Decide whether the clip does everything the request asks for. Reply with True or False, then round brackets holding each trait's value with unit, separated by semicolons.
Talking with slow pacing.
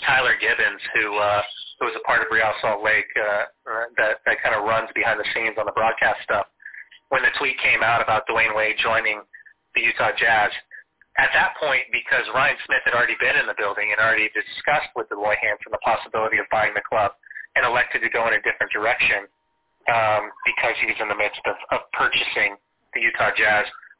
False (205 wpm)